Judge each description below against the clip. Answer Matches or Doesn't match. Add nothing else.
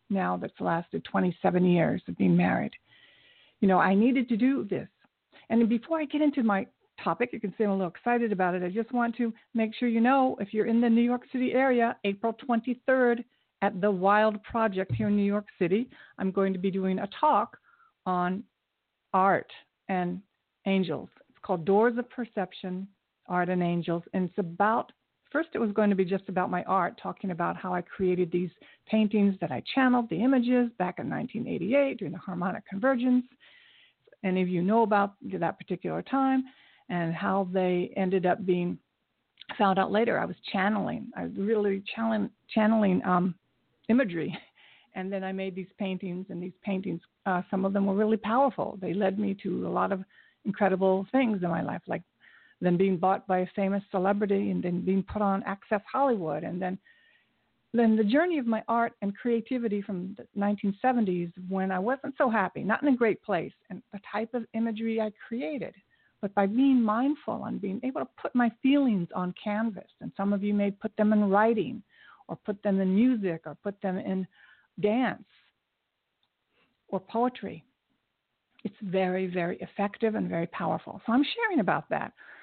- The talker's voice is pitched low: Doesn't match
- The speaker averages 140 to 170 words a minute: Doesn't match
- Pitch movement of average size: Matches